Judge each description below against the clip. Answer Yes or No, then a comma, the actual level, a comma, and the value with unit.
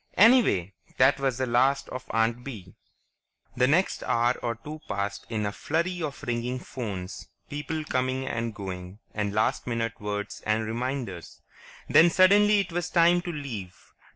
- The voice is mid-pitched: No, low, 125 Hz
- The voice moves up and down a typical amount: No, wide, 6.0 semitones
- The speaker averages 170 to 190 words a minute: No, average, 155 wpm